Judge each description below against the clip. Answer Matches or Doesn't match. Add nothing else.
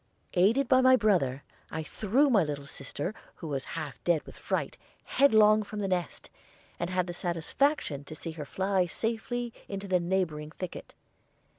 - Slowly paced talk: Doesn't match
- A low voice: Doesn't match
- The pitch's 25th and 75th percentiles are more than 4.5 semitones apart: Matches